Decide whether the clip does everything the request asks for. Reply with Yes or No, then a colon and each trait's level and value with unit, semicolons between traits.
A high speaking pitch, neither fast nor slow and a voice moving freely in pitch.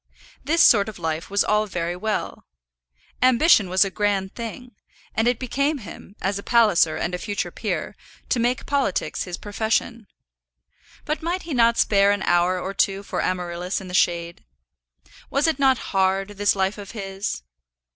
No: high, 205 Hz; average, 170 wpm; average, 4.1 semitones